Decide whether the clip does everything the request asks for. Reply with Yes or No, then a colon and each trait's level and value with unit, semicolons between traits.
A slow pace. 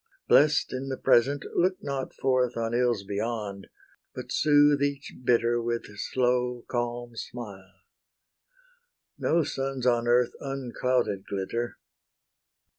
Yes: slow, 115 wpm